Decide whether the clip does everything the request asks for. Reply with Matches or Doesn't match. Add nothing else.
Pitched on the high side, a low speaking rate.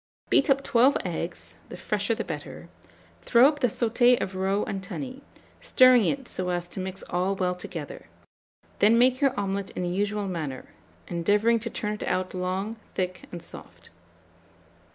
Doesn't match